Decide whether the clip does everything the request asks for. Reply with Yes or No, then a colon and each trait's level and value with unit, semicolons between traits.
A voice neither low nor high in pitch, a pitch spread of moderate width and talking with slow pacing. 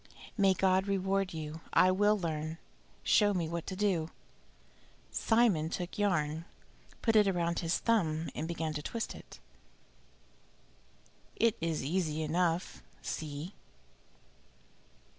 Yes: medium, 175 Hz; average, 3.6 semitones; slow, 120 wpm